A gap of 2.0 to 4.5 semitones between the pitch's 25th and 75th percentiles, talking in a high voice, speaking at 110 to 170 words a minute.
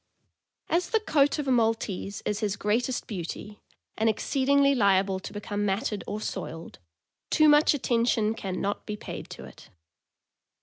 No: average, 5.2 semitones; high, 215 Hz; average, 150 wpm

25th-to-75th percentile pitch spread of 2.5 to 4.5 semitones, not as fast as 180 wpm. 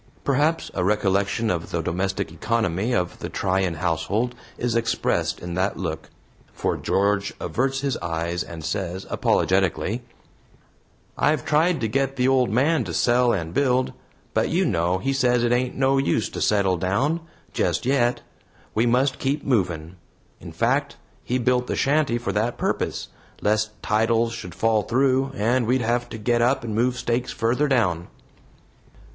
No: average, 5.2 semitones; average, 160 wpm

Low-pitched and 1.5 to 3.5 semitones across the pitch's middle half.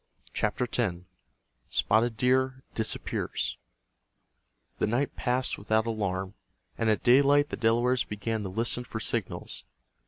Yes: low, 115 Hz; average, 3.0 semitones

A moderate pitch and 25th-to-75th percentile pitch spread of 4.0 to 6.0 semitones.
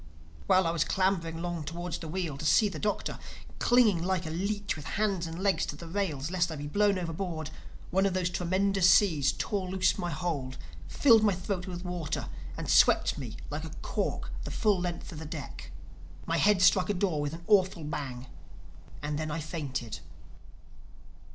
No: medium, 175 Hz; average, 3.5 semitones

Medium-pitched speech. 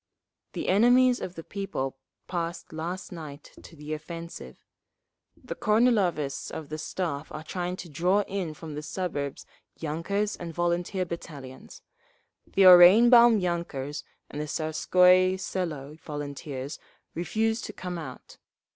Yes: medium, 170 Hz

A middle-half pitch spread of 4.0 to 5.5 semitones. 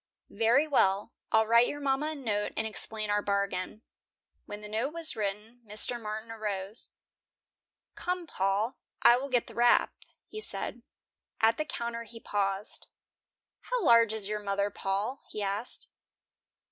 No: average, 3.0 semitones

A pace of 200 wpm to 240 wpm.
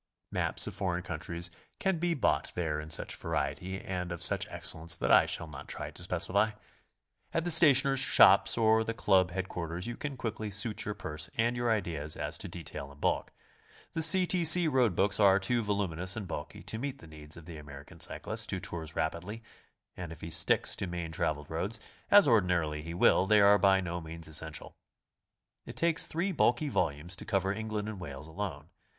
Yes: fast, 205 wpm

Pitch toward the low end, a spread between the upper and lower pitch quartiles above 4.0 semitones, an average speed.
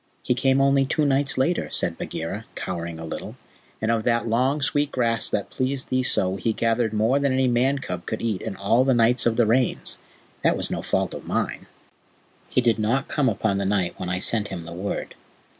No: low, 115 Hz; average, 4.5 semitones; fast, 215 wpm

